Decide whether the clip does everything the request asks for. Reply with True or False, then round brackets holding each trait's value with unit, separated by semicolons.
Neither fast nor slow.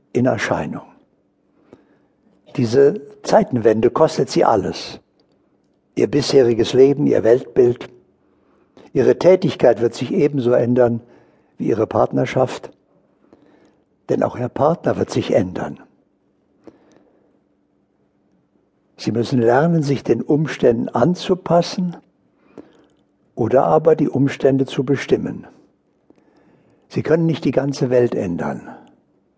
False (100 wpm)